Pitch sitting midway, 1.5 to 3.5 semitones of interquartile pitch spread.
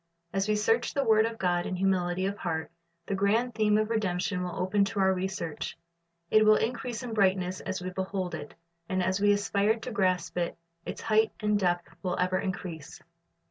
No: high, 195 Hz; average, 2.8 semitones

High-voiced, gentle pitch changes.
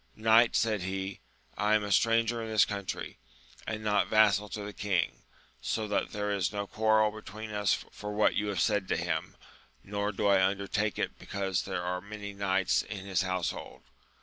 No: low, 105 Hz; narrow, 1.8 semitones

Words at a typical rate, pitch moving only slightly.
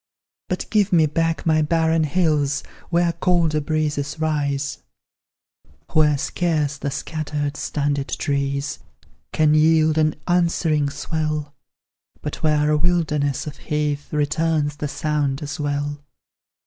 No: slow, 120 wpm; narrow, 1.7 semitones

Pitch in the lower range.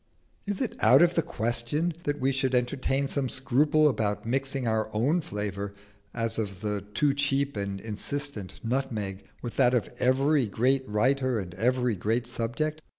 Yes: low, 125 Hz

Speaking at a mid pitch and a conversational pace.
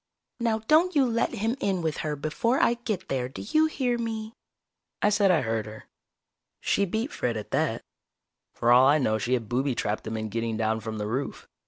No: medium, 150 Hz; fast, 210 wpm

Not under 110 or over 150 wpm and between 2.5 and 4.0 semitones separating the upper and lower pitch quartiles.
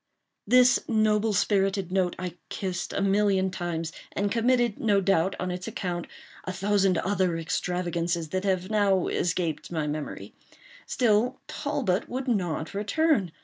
Yes: average, 140 wpm; average, 2.9 semitones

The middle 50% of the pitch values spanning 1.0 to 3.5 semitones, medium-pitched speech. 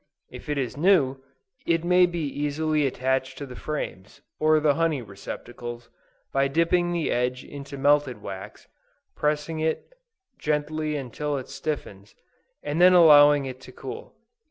Yes: average, 3.0 semitones; medium, 145 Hz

